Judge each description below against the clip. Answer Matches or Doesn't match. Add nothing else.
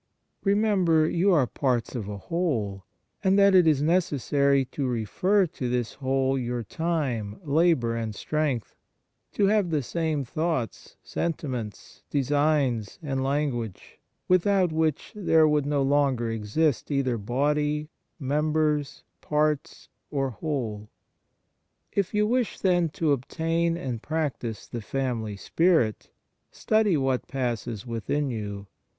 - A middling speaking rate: Doesn't match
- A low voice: Doesn't match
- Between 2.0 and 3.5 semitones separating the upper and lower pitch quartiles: Doesn't match